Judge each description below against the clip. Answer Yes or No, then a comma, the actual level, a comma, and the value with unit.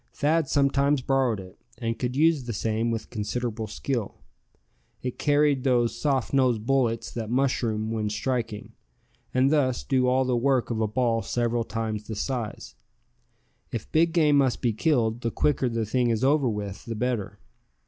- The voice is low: Yes, low, 120 Hz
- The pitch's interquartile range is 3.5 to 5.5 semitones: No, average, 3.1 semitones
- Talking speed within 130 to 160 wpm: No, average, 170 wpm